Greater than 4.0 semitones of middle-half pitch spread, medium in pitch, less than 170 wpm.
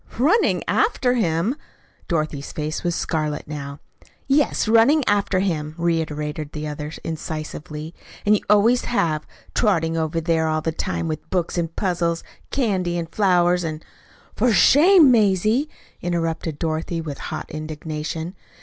Yes: average, 4.7 semitones; medium, 165 Hz; average, 140 wpm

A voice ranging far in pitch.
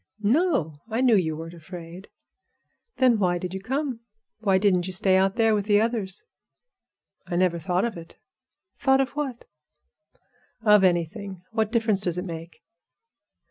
No: average, 4.2 semitones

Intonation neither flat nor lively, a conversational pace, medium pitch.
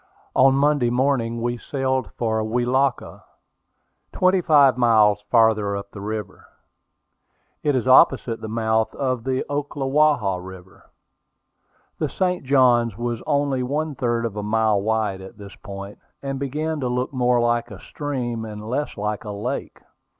No: average, 3.8 semitones; average, 150 wpm; low, 120 Hz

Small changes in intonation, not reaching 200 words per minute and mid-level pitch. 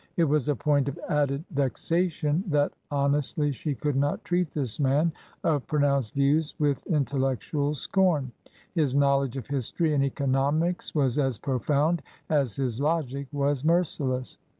Yes: narrow, 1.9 semitones; average, 150 wpm; medium, 145 Hz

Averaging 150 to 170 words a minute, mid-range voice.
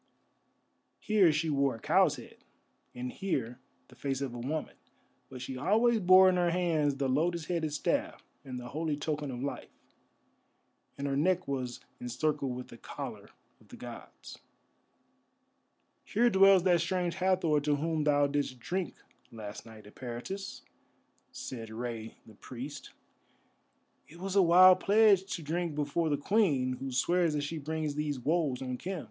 Yes: average, 160 wpm; medium, 150 Hz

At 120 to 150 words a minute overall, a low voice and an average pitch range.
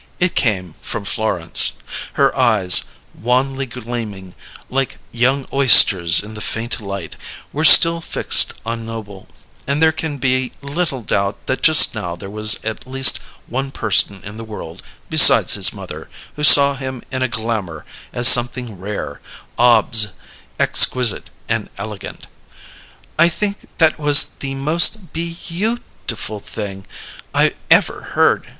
Yes: average, 140 wpm; low, 120 Hz; average, 4.8 semitones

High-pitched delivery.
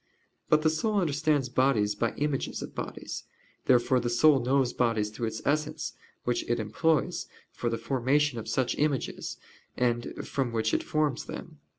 No: low, 130 Hz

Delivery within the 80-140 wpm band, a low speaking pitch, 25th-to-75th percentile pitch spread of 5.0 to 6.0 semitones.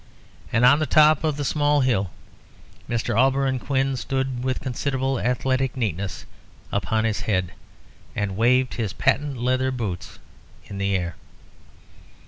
No: slow, 135 wpm; low, 125 Hz; average, 4.2 semitones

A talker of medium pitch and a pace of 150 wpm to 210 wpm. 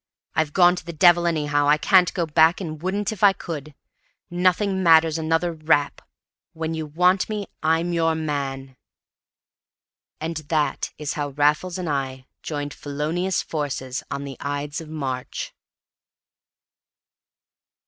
No: medium, 160 Hz; average, 140 wpm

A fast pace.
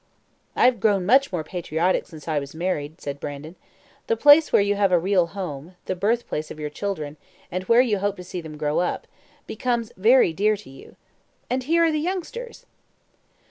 No: average, 195 wpm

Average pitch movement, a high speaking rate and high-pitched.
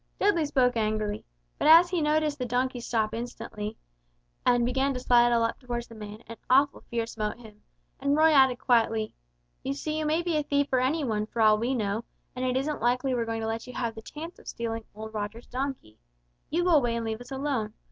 Yes: average, 3.9 semitones; fast, 220 wpm; high, 245 Hz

